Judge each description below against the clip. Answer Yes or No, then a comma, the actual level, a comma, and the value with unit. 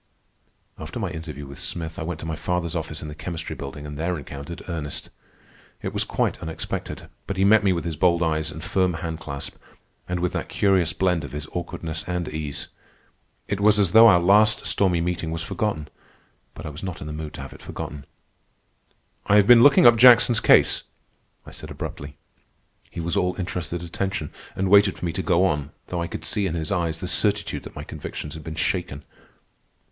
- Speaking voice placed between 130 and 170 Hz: No, very low, 85 Hz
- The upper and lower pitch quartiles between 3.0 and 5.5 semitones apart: Yes, average, 3.4 semitones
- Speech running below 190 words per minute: No, fast, 205 wpm